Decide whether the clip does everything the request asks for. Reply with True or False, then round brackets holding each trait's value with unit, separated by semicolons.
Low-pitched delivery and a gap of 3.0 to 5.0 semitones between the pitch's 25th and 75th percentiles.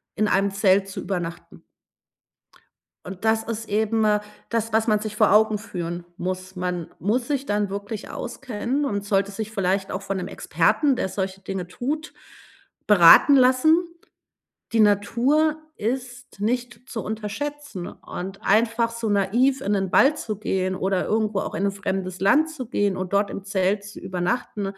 False (210 Hz; 3.3 semitones)